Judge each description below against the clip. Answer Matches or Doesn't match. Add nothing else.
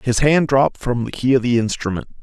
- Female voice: Doesn't match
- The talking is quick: Matches